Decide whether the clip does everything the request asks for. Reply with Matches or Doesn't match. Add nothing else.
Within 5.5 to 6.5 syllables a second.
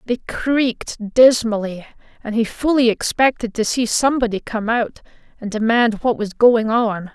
Doesn't match